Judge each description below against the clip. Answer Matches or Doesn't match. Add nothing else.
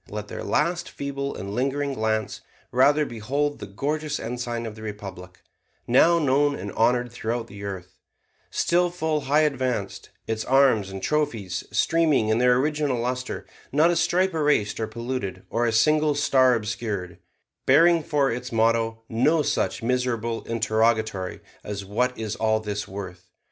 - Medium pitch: Doesn't match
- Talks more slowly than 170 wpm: Matches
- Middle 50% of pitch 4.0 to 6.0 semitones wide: Matches